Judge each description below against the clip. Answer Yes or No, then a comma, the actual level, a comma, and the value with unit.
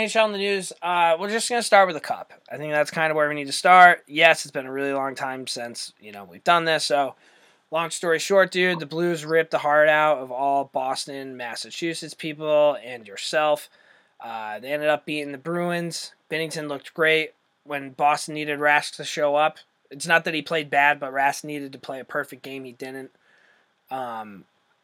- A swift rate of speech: Yes, fast, 215 wpm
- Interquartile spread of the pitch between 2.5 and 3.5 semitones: Yes, average, 3.0 semitones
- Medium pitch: Yes, medium, 150 Hz